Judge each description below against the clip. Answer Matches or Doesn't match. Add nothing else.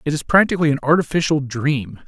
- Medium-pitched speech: Matches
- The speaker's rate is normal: Matches